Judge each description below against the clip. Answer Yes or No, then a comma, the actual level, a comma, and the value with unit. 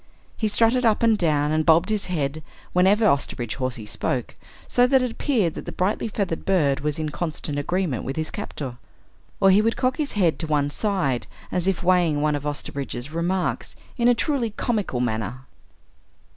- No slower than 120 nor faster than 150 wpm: No, average, 185 wpm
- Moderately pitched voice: Yes, medium, 170 Hz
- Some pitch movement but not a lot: No, wide, 6.5 semitones